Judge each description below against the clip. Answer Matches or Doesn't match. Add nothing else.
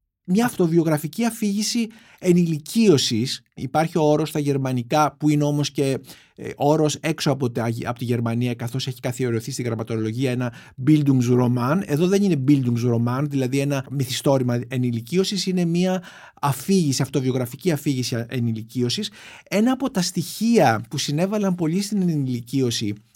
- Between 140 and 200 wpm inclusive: Doesn't match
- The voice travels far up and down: Matches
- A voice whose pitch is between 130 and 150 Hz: Matches